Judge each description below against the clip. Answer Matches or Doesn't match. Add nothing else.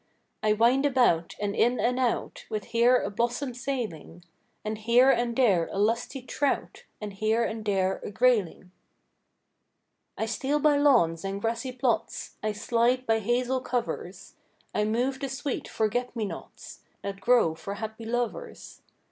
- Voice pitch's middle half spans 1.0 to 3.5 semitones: Matches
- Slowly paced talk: Doesn't match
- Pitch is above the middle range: Matches